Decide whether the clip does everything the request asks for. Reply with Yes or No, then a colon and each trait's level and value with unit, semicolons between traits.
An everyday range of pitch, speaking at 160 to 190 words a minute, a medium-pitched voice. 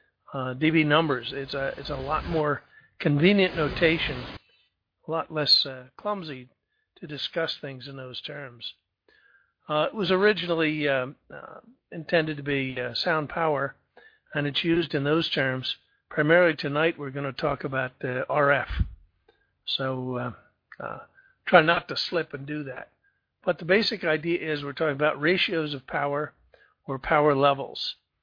No: average, 3.2 semitones; average, 150 wpm; medium, 150 Hz